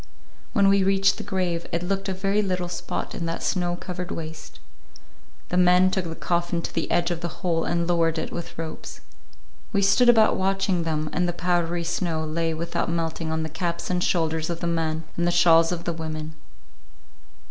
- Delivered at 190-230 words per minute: Yes, average, 200 wpm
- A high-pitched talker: No, medium, 170 Hz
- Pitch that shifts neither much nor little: No, narrow, 1.8 semitones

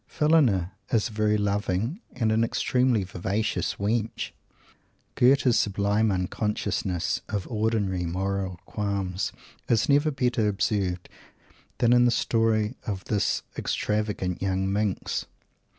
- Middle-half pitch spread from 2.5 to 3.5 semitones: Yes, average, 2.9 semitones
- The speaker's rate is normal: No, slow, 115 wpm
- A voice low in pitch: Yes, low, 105 Hz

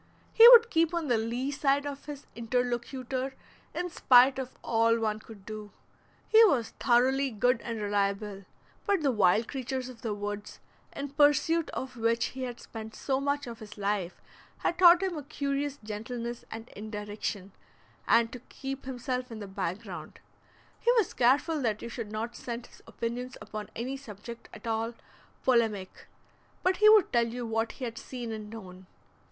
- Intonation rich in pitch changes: No, average, 3.9 semitones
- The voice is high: Yes, high, 240 Hz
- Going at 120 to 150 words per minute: No, average, 175 wpm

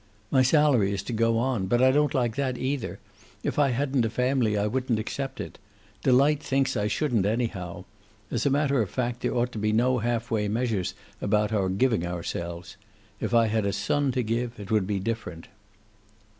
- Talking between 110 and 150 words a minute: No, average, 200 wpm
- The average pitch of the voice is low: Yes, low, 115 Hz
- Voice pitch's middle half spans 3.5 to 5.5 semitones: Yes, average, 3.9 semitones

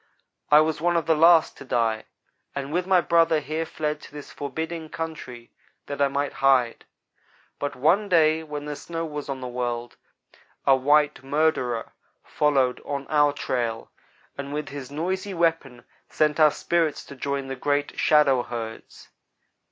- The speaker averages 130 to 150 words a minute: No, average, 160 wpm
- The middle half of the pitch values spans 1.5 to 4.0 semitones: Yes, average, 3.0 semitones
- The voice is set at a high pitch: No, medium, 145 Hz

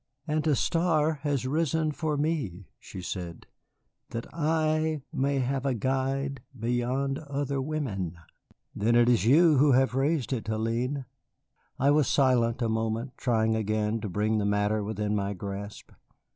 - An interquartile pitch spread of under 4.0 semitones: No, average, 4.8 semitones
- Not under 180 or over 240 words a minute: No, average, 150 wpm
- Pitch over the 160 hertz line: No, low, 130 Hz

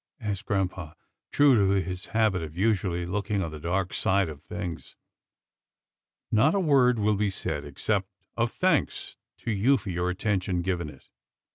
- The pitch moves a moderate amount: Yes, average, 3.7 semitones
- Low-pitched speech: Yes, very low, 95 Hz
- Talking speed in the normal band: Yes, average, 160 wpm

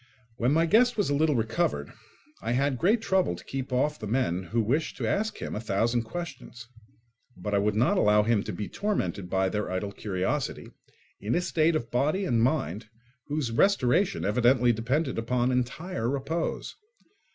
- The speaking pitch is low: Yes, low, 125 Hz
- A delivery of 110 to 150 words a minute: No, average, 175 wpm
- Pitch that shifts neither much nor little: No, wide, 6.6 semitones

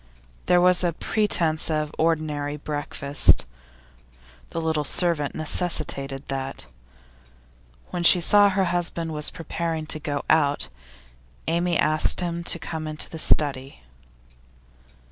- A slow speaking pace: Yes, slow, 115 wpm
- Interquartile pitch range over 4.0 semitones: No, narrow, 2.6 semitones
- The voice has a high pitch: No, medium, 160 Hz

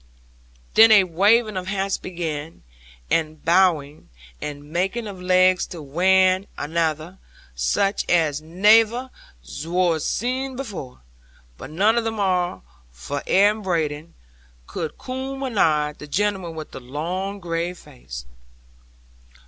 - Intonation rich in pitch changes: No, average, 4.6 semitones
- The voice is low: No, medium, 180 Hz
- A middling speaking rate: No, slow, 125 wpm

